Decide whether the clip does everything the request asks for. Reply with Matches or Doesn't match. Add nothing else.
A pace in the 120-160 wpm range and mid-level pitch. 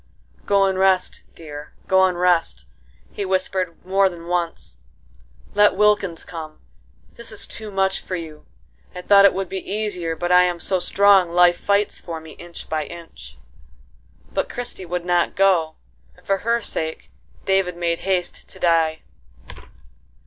Matches